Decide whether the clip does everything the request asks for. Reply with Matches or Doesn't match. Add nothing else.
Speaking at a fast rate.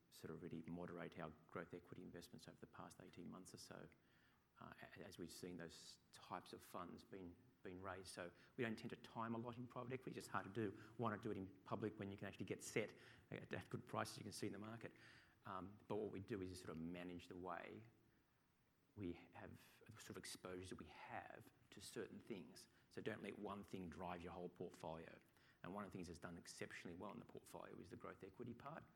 Matches